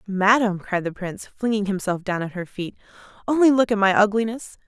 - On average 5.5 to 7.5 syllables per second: Yes, 5.6 syllables/s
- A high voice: Yes, high, 205 Hz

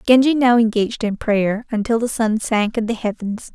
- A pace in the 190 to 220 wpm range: Yes, fast, 205 wpm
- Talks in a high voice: Yes, high, 230 Hz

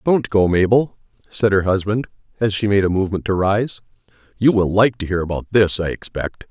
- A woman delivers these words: No, male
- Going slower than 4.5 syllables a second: No, 5.4 syllables/s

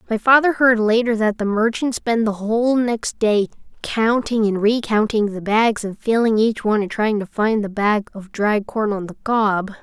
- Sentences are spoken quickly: No, average, 195 wpm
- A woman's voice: Yes, female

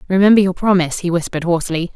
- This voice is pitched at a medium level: Yes, medium, 180 Hz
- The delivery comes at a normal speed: Yes, average, 185 wpm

